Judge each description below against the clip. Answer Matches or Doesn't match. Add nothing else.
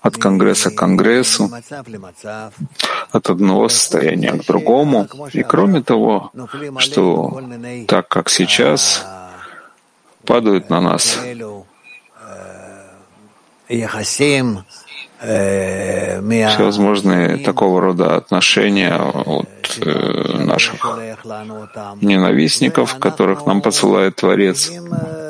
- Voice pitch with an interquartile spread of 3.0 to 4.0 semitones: Matches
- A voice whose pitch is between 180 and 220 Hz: Doesn't match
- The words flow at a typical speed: Doesn't match